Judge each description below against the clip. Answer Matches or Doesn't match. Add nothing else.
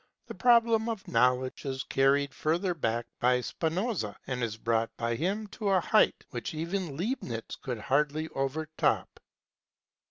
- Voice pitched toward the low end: Doesn't match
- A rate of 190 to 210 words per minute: Doesn't match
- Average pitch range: Doesn't match